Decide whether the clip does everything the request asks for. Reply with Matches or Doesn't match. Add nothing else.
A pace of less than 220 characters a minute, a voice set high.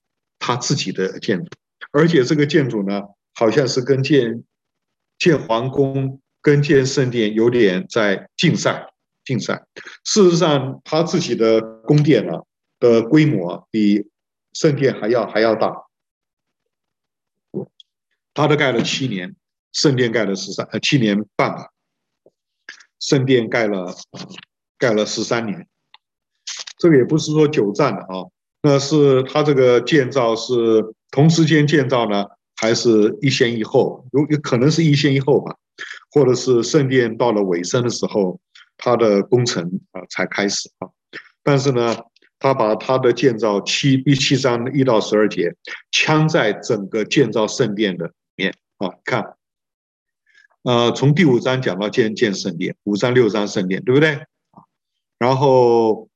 Doesn't match